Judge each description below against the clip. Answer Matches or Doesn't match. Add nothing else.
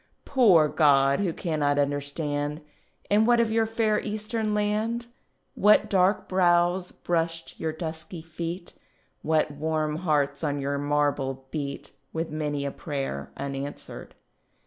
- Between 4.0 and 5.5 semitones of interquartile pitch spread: Matches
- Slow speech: Matches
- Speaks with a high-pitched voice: Doesn't match